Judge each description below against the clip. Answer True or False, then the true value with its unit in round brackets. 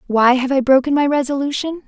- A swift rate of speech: False (190 wpm)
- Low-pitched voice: False (270 Hz)